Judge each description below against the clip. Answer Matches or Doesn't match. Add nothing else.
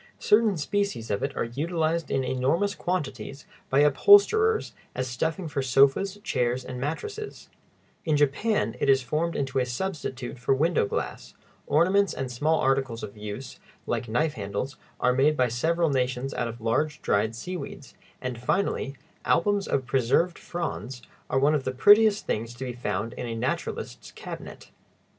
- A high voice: Doesn't match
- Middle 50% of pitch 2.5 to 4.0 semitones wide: Doesn't match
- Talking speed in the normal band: Matches